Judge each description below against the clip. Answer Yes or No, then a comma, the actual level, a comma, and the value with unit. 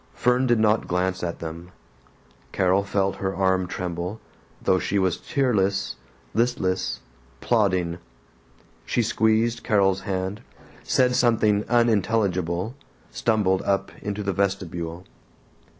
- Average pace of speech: No, slow, 110 wpm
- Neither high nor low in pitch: No, low, 100 Hz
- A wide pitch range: No, average, 3.1 semitones